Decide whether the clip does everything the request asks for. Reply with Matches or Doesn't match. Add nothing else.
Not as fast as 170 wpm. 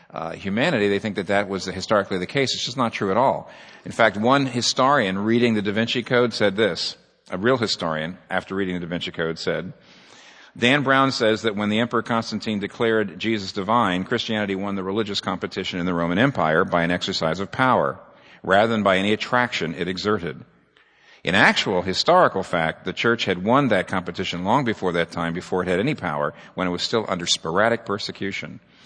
Doesn't match